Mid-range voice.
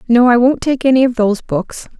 No: high, 240 Hz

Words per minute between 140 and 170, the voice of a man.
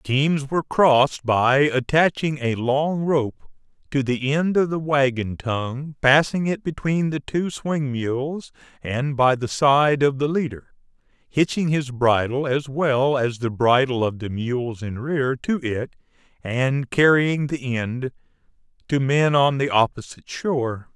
Yes: average, 155 wpm; male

